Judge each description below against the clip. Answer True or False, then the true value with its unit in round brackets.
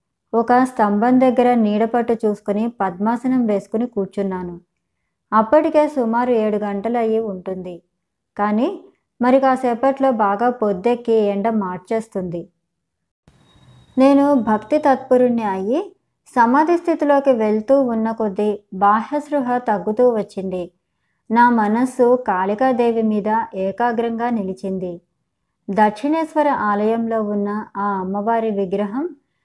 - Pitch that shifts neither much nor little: True (3.6 semitones)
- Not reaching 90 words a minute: False (95 wpm)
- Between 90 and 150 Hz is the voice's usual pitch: False (225 Hz)